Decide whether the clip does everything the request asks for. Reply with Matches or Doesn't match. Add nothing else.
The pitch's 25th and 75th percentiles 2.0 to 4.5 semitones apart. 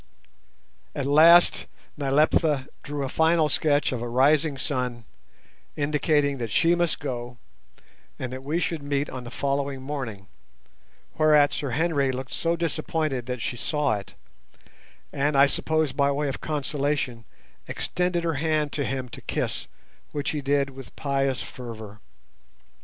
Matches